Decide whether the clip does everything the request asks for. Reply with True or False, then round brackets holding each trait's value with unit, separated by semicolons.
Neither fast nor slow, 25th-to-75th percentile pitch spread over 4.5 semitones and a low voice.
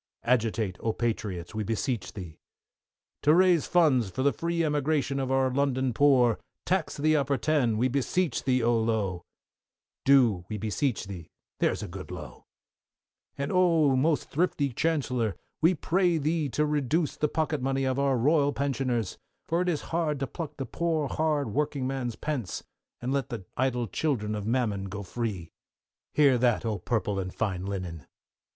True (165 wpm; 5.1 semitones; 130 Hz)